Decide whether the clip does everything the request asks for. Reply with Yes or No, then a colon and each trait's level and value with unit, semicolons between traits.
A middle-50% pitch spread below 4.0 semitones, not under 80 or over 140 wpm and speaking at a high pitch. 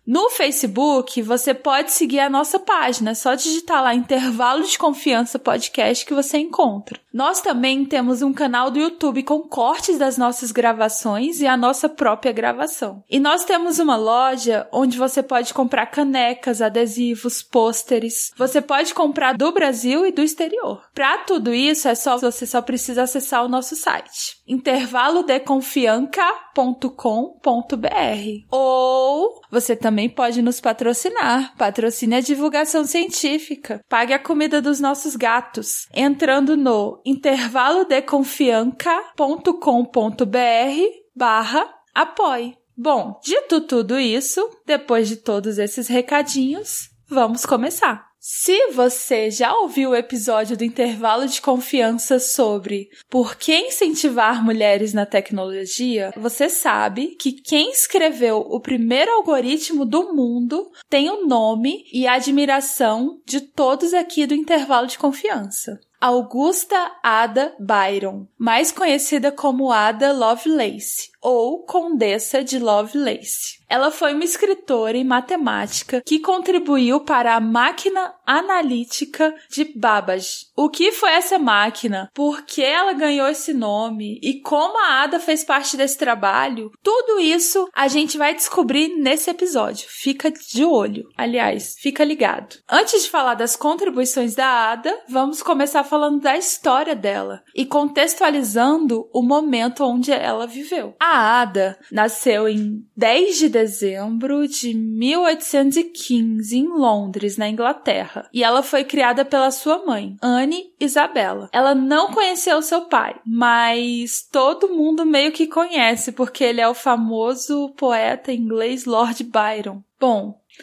No: average, 4.3 semitones; average, 130 wpm; very high, 265 Hz